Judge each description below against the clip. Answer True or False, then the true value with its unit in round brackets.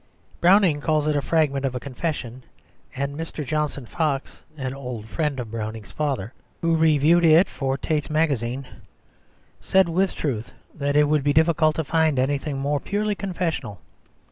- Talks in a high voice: False (145 Hz)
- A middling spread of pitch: True (3.2 semitones)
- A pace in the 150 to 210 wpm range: True (160 wpm)